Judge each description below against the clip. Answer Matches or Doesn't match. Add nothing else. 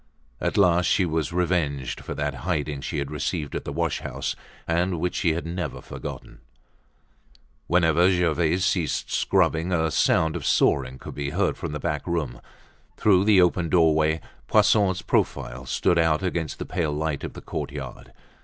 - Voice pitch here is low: Matches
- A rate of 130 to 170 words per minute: Matches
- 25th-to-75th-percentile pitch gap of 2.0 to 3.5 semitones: Matches